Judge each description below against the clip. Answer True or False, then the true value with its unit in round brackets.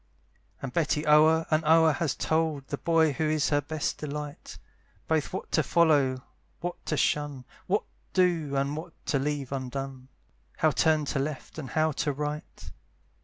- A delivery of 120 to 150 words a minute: False (165 wpm)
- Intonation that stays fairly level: True (2.3 semitones)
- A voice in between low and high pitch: True (150 Hz)